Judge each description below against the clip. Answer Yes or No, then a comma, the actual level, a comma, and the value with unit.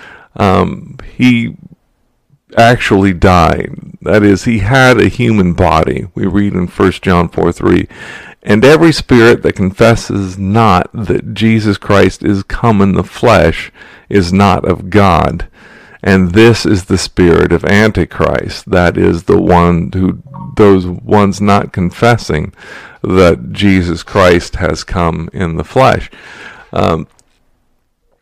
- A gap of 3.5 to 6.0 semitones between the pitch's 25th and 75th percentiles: Yes, average, 3.9 semitones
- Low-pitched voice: Yes, low, 100 Hz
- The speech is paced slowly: Yes, slow, 130 wpm